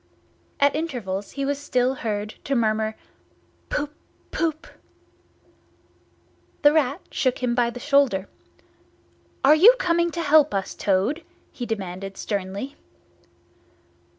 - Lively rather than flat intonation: Yes, wide, 5.7 semitones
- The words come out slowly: Yes, slow, 115 wpm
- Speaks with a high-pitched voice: Yes, very high, 255 Hz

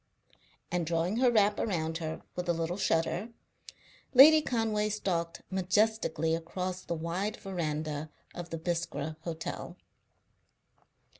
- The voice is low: No, medium, 175 Hz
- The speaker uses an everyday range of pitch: Yes, average, 4.1 semitones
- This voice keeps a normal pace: No, slow, 120 wpm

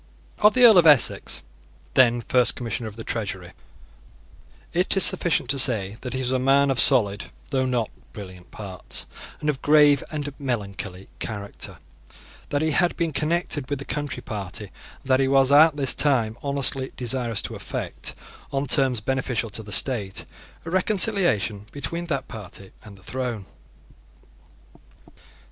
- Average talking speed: Yes, average, 160 wpm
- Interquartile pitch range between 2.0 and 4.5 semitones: No, average, 5.0 semitones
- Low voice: Yes, low, 130 Hz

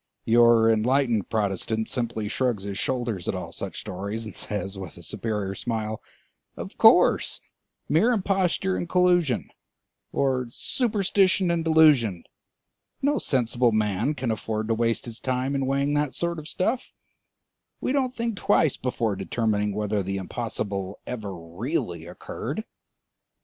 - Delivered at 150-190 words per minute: No, average, 140 wpm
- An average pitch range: No, wide, 6.6 semitones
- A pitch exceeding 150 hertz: No, low, 120 Hz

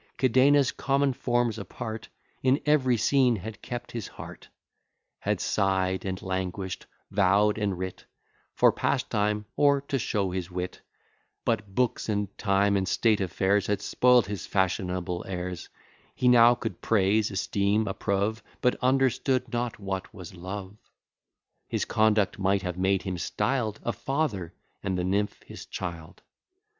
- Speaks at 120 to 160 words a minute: Yes, average, 140 wpm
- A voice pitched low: Yes, low, 105 Hz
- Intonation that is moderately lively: Yes, average, 4.2 semitones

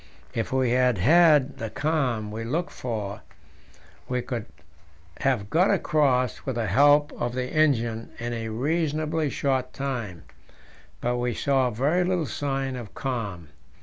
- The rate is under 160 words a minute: Yes, average, 145 wpm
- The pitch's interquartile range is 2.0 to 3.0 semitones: No, average, 4.1 semitones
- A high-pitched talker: No, low, 130 Hz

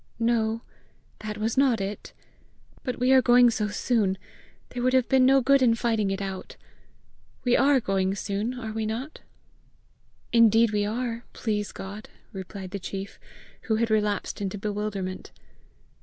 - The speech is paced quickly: No, average, 155 wpm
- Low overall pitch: No, high, 220 Hz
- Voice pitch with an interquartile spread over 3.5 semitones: No, average, 3.2 semitones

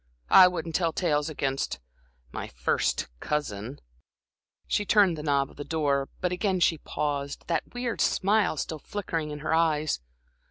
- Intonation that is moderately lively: Yes, average, 3.8 semitones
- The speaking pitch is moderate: Yes, medium, 155 Hz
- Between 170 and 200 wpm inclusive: No, average, 155 wpm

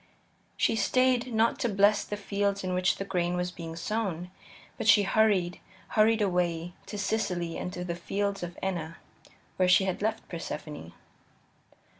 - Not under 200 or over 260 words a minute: No, average, 160 wpm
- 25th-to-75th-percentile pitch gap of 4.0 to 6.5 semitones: No, average, 3.1 semitones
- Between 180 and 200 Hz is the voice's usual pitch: Yes, high, 190 Hz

